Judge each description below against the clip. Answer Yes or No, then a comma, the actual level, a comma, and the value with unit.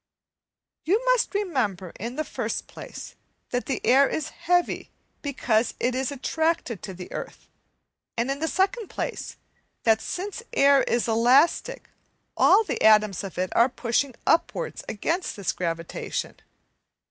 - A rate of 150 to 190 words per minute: No, average, 140 wpm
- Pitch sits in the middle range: No, very high, 265 Hz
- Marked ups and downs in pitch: Yes, wide, 7.2 semitones